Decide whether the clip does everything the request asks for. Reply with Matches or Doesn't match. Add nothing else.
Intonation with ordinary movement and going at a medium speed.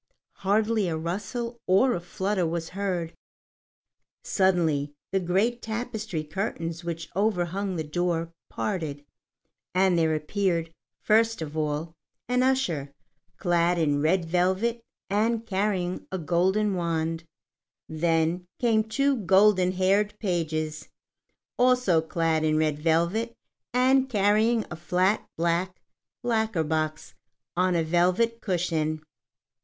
Doesn't match